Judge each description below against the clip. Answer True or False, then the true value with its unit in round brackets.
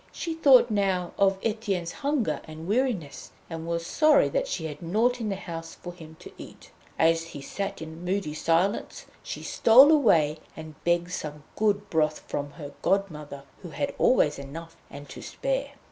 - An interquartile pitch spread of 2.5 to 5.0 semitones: False (5.4 semitones)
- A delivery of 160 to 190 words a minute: True (175 wpm)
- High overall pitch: False (175 Hz)